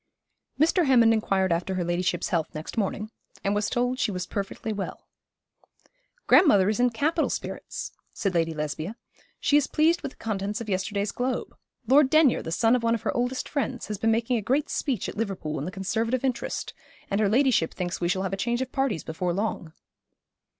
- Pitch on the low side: No, high, 215 Hz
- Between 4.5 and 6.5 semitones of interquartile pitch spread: Yes, average, 4.9 semitones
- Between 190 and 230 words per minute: Yes, average, 200 wpm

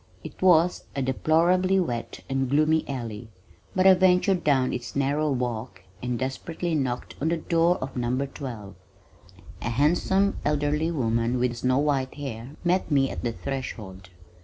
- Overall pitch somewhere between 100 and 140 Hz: Yes, low, 135 Hz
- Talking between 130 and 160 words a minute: Yes, average, 155 wpm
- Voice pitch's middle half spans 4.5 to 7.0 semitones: Yes, average, 4.9 semitones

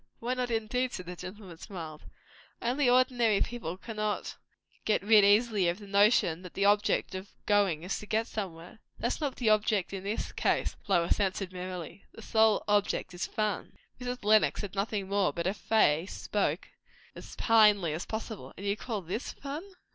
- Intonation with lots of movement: No, average, 3.2 semitones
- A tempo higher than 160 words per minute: Yes, average, 180 wpm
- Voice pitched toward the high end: Yes, high, 205 Hz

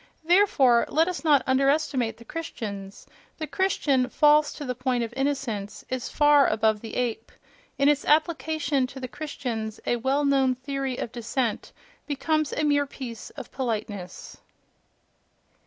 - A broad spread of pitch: No, average, 3.9 semitones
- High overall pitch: Yes, very high, 265 Hz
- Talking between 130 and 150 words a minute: Yes, average, 140 wpm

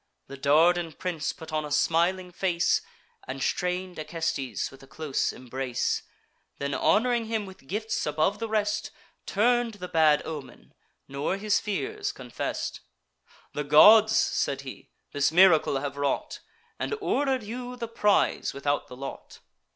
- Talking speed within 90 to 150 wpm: Yes, average, 145 wpm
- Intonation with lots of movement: Yes, wide, 6.6 semitones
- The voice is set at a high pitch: No, medium, 175 Hz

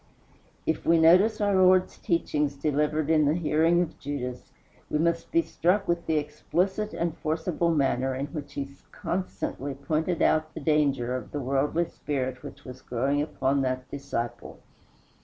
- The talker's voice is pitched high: No, medium, 150 Hz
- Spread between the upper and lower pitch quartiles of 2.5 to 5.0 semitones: Yes, average, 3.5 semitones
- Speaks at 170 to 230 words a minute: No, average, 160 wpm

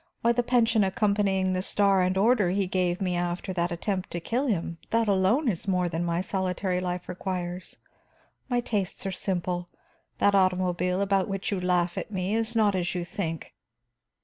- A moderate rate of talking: Yes, average, 180 wpm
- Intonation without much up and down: Yes, narrow, 2.2 semitones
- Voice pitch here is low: No, medium, 185 Hz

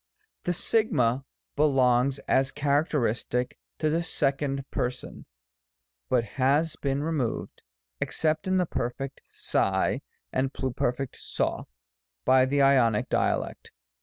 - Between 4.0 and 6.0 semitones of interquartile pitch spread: No, average, 2.7 semitones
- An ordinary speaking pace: No, slow, 110 wpm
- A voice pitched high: No, low, 135 Hz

